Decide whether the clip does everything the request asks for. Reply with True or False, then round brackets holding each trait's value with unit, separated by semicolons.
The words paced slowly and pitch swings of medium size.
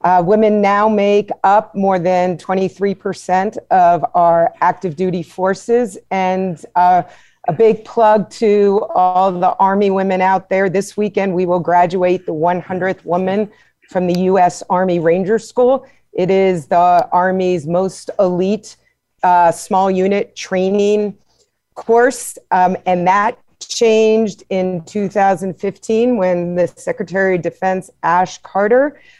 False (130 wpm; 2.2 semitones)